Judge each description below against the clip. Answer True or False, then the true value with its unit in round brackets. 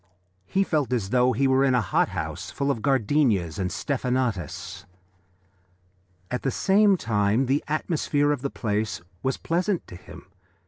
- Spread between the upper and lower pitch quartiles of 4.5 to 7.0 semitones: True (5.2 semitones)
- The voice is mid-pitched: False (130 Hz)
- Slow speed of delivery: False (155 wpm)